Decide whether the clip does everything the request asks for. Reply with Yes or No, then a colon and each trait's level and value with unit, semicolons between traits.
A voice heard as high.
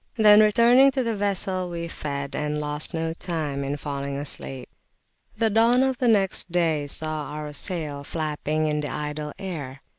No: medium, 155 Hz